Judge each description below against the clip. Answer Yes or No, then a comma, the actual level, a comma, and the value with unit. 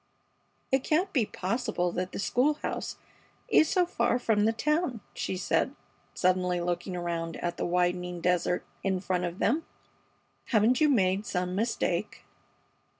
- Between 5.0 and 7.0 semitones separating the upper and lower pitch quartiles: Yes, wide, 5.6 semitones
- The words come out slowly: No, average, 150 wpm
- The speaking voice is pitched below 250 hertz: Yes, high, 190 Hz